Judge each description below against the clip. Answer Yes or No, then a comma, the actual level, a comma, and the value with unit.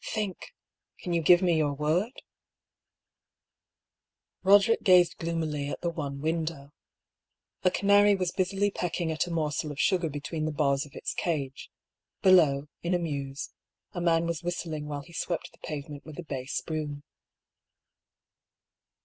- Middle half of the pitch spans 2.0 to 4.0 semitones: Yes, average, 3.3 semitones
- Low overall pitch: No, medium, 165 Hz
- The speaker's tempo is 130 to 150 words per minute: No, average, 160 wpm